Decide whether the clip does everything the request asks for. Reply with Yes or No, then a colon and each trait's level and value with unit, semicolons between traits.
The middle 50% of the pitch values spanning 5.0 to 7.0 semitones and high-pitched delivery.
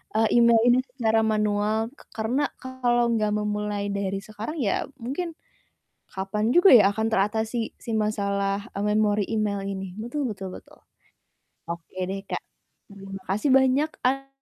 No: average, 3.2 semitones; high, 215 Hz